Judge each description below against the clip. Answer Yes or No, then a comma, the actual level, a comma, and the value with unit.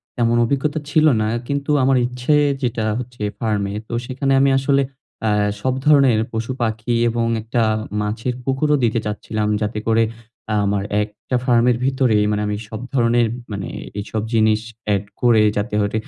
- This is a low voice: Yes, low, 115 Hz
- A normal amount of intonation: Yes, average, 3.3 semitones